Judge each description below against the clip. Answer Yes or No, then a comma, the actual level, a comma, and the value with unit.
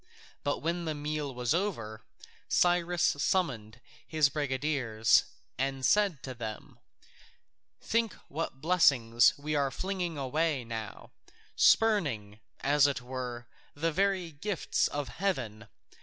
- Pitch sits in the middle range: Yes, medium, 145 Hz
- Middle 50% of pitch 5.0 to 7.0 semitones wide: Yes, wide, 5.6 semitones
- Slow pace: Yes, slow, 115 wpm